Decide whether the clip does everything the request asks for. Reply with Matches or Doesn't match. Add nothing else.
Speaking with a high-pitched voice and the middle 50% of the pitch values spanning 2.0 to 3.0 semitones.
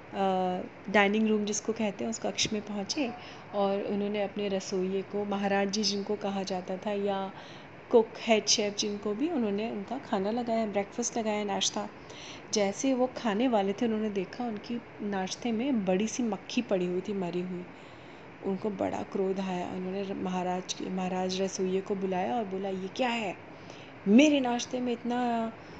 Matches